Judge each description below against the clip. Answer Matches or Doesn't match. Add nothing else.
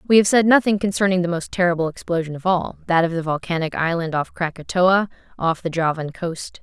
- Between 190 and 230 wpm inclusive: Matches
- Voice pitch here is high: Doesn't match